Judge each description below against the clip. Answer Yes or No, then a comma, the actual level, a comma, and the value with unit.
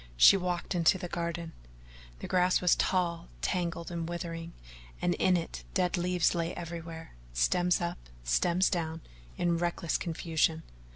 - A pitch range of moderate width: No, narrow, 1.2 semitones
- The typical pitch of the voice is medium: Yes, medium, 170 Hz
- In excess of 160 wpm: No, average, 140 wpm